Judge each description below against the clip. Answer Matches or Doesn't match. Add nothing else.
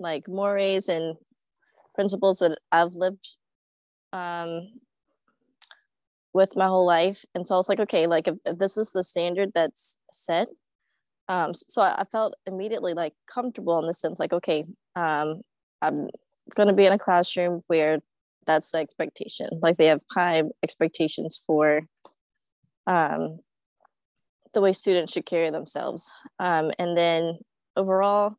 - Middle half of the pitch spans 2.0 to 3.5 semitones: Matches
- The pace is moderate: Matches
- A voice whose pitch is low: Doesn't match